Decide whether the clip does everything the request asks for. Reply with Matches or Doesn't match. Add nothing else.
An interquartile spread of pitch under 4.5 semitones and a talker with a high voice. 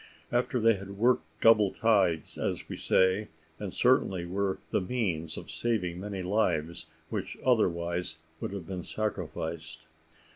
Doesn't match